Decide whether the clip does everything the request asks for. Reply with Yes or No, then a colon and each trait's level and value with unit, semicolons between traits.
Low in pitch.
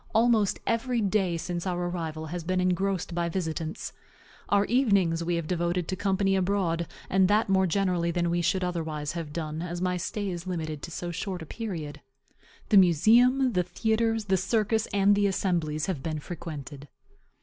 No: medium, 180 Hz